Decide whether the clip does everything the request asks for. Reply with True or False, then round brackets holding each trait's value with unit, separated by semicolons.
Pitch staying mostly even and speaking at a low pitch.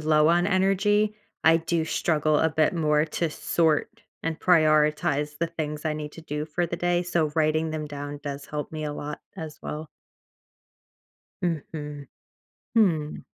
False (2.1 semitones; 155 Hz)